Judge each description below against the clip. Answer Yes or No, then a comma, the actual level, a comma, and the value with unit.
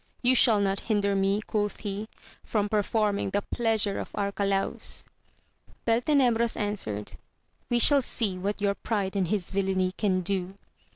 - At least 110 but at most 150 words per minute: Yes, average, 140 wpm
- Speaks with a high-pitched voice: Yes, high, 205 Hz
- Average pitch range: No, narrow, 2.2 semitones